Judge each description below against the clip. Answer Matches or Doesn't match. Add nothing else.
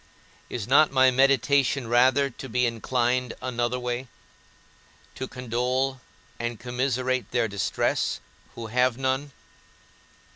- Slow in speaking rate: Matches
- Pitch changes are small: Matches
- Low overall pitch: Matches